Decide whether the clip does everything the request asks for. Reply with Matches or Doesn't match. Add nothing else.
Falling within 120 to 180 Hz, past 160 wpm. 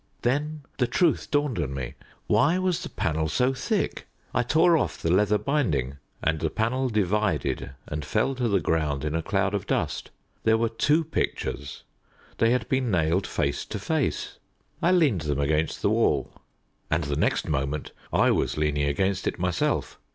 Doesn't match